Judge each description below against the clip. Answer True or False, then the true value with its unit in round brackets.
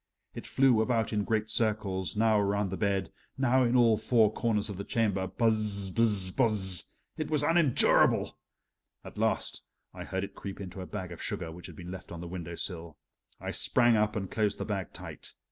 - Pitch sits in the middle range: False (105 Hz)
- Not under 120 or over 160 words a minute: False (195 wpm)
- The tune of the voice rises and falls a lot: False (3.2 semitones)